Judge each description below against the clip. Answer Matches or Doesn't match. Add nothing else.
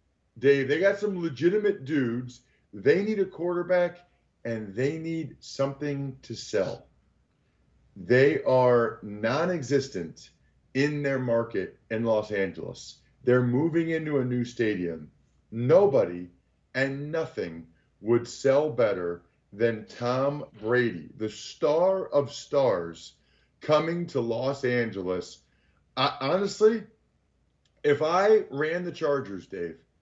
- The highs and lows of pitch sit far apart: Matches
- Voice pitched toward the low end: Matches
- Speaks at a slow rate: Matches